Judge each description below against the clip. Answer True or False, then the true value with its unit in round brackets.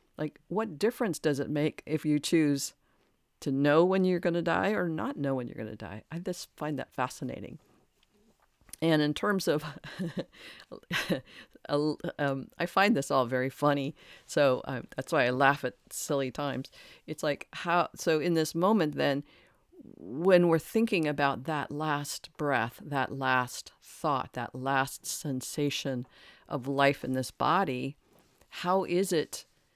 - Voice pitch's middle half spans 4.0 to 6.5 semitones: False (3.6 semitones)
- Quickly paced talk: False (160 wpm)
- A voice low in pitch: False (150 Hz)